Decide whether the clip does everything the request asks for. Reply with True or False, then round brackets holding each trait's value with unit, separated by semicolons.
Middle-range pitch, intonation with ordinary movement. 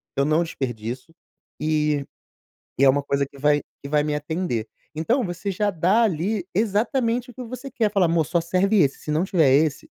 False (165 Hz; 5.8 semitones)